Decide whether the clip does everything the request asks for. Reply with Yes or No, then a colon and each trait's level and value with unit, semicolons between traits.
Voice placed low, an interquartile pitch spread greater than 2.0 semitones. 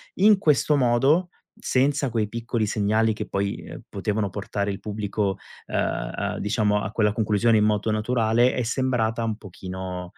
Yes: low, 110 Hz; average, 2.8 semitones